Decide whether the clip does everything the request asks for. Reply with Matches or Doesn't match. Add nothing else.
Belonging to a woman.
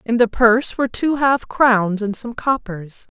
Matches